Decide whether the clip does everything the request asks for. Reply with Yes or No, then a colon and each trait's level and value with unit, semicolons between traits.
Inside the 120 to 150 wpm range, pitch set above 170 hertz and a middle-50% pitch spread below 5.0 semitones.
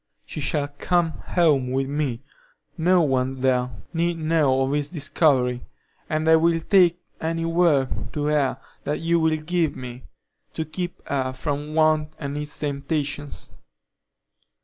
No: average, 145 wpm; medium, 150 Hz; average, 3.1 semitones